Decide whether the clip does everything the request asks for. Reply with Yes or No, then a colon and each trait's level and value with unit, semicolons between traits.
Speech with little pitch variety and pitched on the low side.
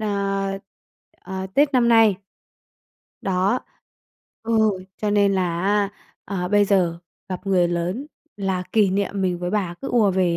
No: narrow, 2.3 semitones; high, 195 Hz